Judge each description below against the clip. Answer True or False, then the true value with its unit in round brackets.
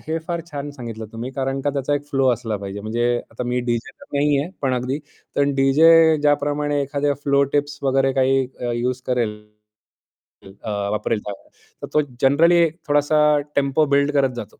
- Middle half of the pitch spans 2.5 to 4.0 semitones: True (3.0 semitones)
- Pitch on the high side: False (135 Hz)